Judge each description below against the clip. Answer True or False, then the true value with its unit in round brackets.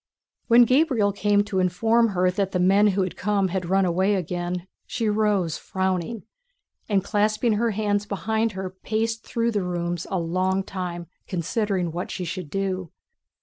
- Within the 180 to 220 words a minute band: False (165 wpm)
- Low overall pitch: False (195 Hz)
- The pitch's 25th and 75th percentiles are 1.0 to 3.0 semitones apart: True (2.7 semitones)